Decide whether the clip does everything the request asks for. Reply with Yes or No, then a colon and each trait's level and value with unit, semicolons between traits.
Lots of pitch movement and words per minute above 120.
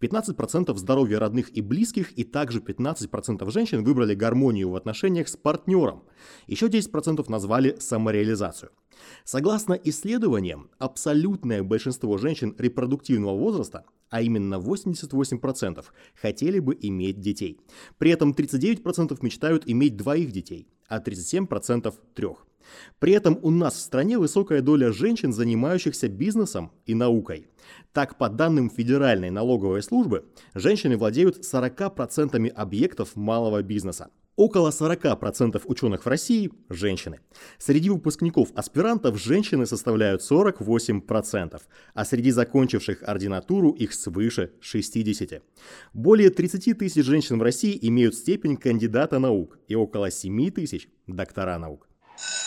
No: wide, 6.8 semitones; average, 115 wpm